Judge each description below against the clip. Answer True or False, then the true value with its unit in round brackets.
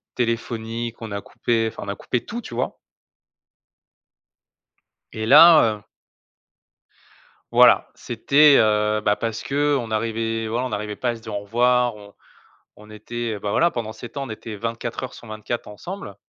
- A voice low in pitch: True (115 Hz)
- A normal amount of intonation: False (2.3 semitones)